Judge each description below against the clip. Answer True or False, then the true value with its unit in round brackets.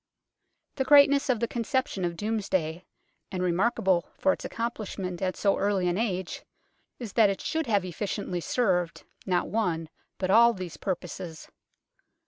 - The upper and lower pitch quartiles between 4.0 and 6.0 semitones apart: True (4.4 semitones)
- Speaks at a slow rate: False (145 wpm)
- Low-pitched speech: False (195 Hz)